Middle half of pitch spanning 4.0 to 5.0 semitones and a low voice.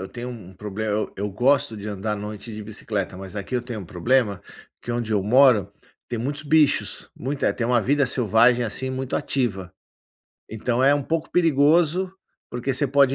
Yes: average, 4.5 semitones; low, 120 Hz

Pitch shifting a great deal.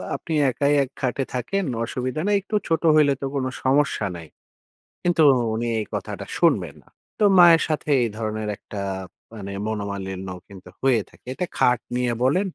Yes: wide, 6.2 semitones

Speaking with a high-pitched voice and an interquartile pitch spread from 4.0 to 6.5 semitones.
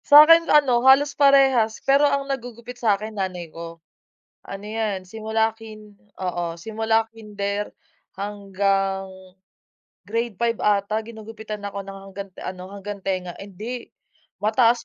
No: high, 215 Hz; average, 2.9 semitones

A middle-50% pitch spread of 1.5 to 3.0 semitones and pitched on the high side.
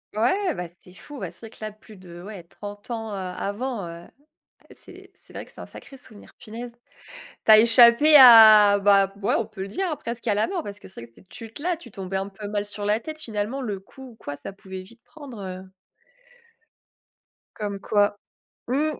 No: average, 3.6 semitones; high, 210 Hz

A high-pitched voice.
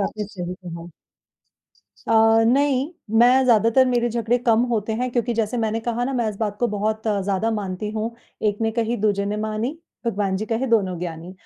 Yes: high, 220 Hz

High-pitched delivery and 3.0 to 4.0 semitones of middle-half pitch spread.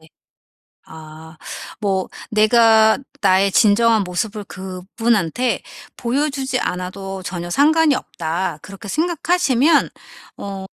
No: high, 205 Hz; average, 5.1 semitones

